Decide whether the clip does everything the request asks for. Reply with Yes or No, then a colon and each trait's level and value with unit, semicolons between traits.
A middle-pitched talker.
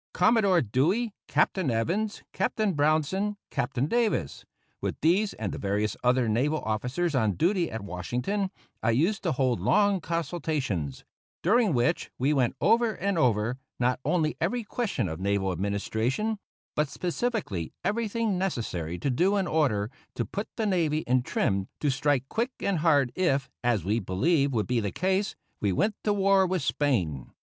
Yes: medium, 145 Hz